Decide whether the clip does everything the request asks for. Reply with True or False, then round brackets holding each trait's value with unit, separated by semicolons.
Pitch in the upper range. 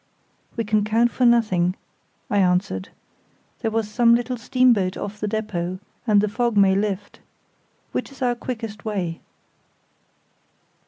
True (215 Hz)